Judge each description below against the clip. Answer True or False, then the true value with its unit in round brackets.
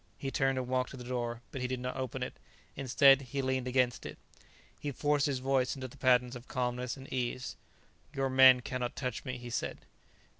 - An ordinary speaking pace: False (210 wpm)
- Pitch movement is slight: True (1.2 semitones)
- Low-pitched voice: True (130 Hz)